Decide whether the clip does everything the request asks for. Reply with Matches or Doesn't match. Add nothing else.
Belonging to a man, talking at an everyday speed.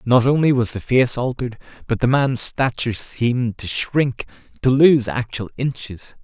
Matches